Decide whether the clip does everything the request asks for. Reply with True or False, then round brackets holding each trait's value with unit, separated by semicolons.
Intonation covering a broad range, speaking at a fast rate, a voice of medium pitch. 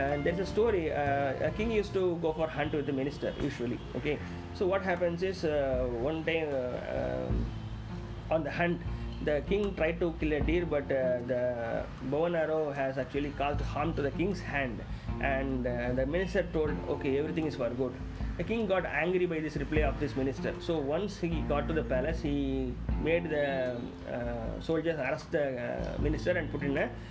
False (4.5 semitones; 200 wpm; 145 Hz)